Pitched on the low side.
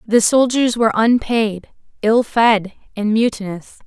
No: high, 220 Hz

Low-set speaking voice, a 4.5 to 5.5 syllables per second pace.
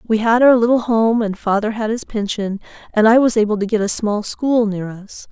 No: high, 220 Hz; 5.1 syllables/s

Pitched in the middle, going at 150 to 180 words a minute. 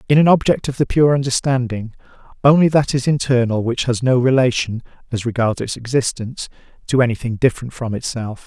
No: low, 125 Hz; average, 170 wpm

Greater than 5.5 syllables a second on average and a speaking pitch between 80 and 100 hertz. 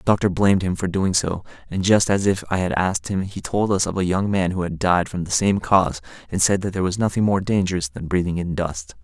Yes: 6.0 syllables/s; very low, 90 Hz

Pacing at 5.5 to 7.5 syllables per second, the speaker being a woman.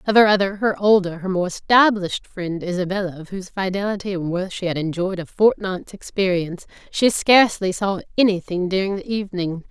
Yes: 5.7 syllables/s; female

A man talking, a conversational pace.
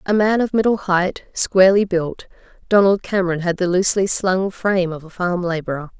No: female; average, 180 wpm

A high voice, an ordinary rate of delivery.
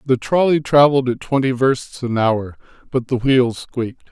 No: low, 125 Hz; average, 175 wpm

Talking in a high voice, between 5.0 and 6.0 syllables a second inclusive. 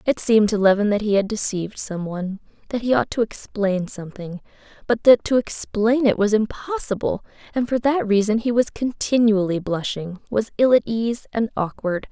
Yes: high, 215 Hz; 5.2 syllables/s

